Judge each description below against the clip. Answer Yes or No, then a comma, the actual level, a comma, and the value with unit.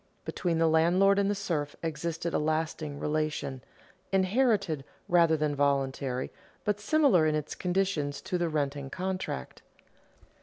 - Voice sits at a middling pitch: Yes, medium, 160 Hz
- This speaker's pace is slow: Yes, slow, 130 wpm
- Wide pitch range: No, average, 4.4 semitones